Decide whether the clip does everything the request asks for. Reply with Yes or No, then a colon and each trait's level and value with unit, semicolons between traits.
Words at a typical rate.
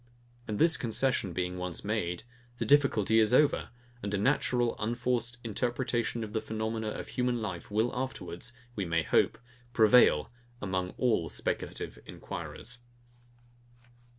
No: slow, 130 wpm